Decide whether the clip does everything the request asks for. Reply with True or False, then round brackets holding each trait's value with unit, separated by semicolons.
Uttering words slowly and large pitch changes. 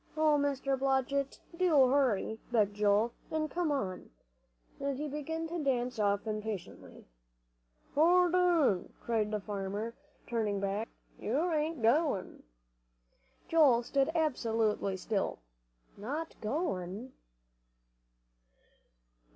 True (100 wpm; 6.3 semitones)